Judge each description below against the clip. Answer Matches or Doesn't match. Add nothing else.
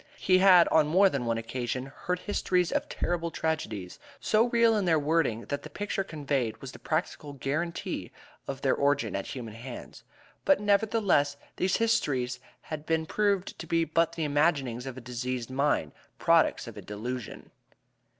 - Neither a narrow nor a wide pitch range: Doesn't match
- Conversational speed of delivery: Matches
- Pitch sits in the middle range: Matches